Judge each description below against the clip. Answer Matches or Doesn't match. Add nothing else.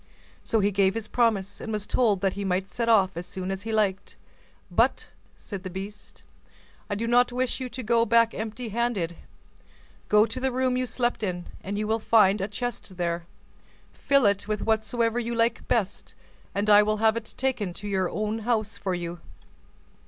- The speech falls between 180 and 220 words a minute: Matches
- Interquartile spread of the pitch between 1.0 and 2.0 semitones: Doesn't match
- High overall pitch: Matches